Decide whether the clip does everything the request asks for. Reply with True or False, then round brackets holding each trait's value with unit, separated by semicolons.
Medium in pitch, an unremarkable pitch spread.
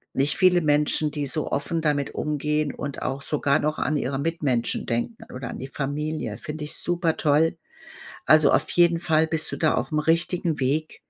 False (150 Hz; 2.1 semitones)